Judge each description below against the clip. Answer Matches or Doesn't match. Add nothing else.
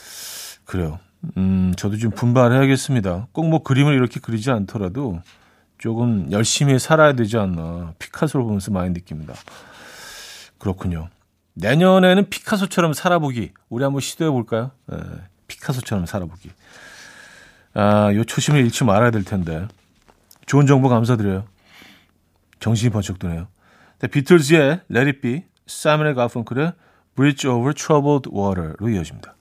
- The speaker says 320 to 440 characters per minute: Matches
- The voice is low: Matches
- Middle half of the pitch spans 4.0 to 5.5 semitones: Doesn't match